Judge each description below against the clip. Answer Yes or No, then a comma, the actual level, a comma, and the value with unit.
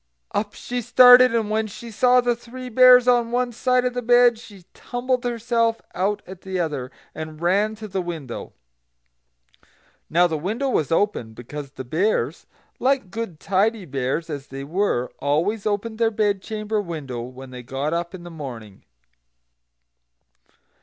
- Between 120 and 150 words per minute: No, average, 160 wpm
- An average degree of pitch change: No, wide, 7.2 semitones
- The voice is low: No, high, 205 Hz